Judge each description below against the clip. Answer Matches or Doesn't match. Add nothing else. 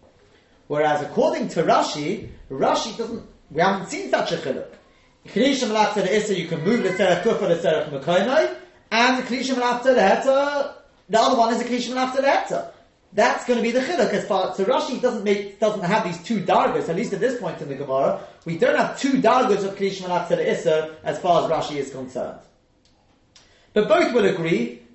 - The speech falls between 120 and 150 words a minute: Doesn't match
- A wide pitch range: Matches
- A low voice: Doesn't match